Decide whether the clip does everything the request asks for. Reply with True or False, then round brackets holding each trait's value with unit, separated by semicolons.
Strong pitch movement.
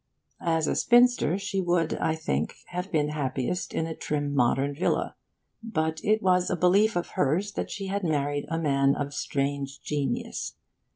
False (4.2 semitones)